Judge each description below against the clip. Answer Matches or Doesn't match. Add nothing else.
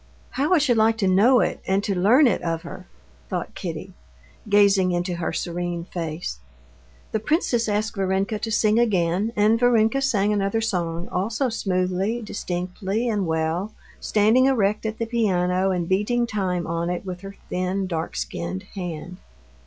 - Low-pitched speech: Doesn't match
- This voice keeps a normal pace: Matches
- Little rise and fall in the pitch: Doesn't match